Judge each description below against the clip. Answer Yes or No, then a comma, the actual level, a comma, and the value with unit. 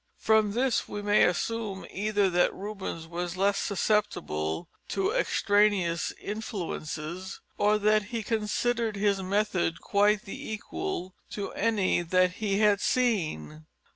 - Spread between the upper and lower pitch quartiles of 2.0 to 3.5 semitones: Yes, average, 2.8 semitones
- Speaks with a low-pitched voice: No, high, 205 Hz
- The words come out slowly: Yes, slow, 125 wpm